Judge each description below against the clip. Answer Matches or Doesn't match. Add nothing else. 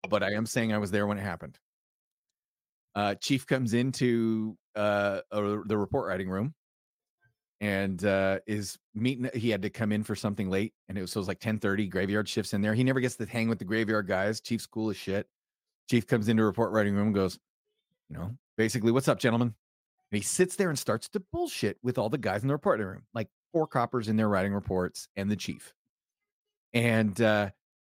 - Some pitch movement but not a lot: Matches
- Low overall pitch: Matches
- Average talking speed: Doesn't match